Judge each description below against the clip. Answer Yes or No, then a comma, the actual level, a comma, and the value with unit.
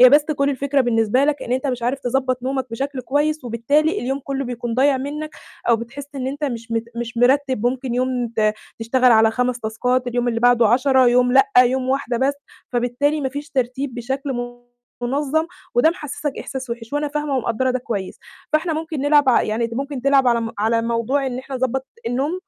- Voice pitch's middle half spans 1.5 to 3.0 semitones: Yes, average, 2.7 semitones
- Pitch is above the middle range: Yes, very high, 255 Hz